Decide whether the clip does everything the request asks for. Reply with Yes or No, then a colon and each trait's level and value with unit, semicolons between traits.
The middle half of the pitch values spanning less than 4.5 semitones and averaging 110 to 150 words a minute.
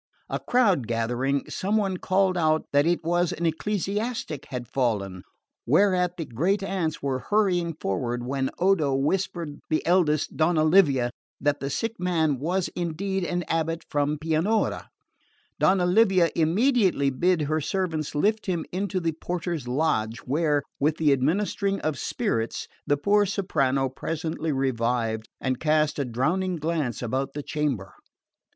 No: average, 5.1 semitones; average, 145 wpm